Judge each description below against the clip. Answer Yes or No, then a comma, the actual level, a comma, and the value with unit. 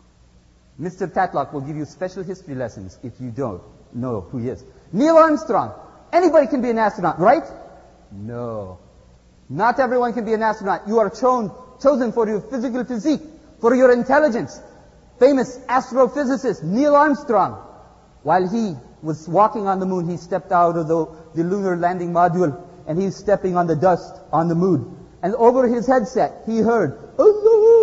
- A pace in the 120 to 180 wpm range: Yes, average, 165 wpm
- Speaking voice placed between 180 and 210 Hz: Yes, high, 190 Hz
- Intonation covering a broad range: Yes, wide, 7.5 semitones